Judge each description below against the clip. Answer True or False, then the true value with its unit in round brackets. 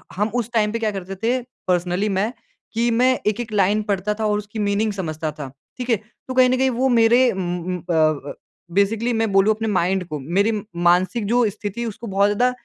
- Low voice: False (210 Hz)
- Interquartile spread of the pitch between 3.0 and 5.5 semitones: True (3.7 semitones)